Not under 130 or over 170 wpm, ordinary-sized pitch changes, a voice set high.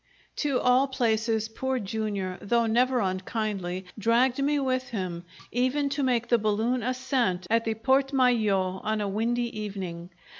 Yes: average, 150 wpm; average, 3.9 semitones; high, 230 Hz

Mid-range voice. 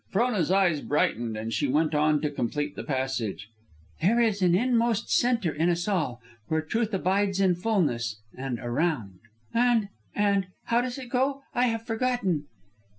Yes: medium, 180 Hz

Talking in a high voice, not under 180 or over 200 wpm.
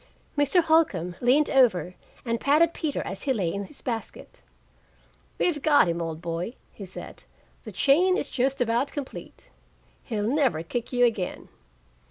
No: high, 245 Hz; average, 155 wpm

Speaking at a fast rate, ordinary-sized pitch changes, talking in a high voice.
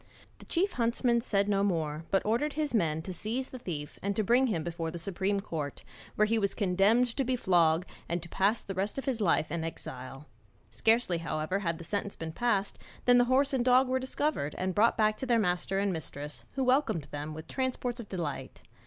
No: fast, 215 wpm; wide, 6.5 semitones; high, 200 Hz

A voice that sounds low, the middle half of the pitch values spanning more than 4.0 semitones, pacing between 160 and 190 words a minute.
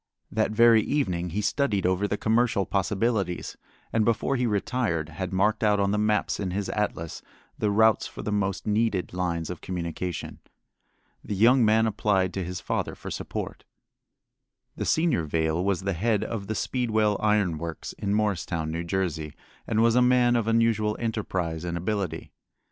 No: low, 105 Hz; average, 3.6 semitones; average, 170 wpm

